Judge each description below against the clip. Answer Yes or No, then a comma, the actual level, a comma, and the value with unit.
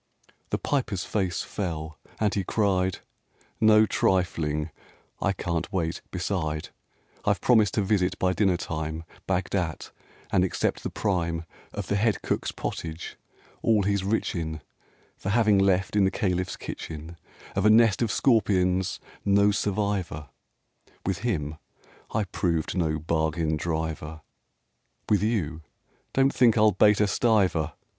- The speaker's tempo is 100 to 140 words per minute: Yes, slow, 135 wpm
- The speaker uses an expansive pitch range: No, average, 4.1 semitones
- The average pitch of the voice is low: Yes, very low, 95 Hz